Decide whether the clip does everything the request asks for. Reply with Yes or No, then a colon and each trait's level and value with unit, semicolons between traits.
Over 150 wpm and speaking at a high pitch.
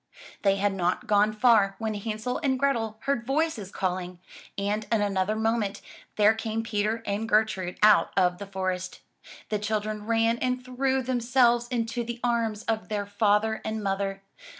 Yes: average, 160 wpm; high, 215 Hz